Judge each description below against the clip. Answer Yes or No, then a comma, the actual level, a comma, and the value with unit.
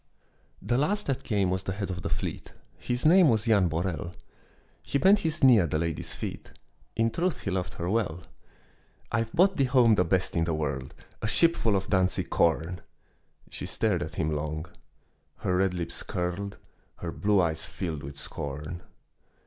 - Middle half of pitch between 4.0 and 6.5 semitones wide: Yes, wide, 5.5 semitones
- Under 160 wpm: No, average, 180 wpm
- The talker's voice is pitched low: Yes, very low, 95 Hz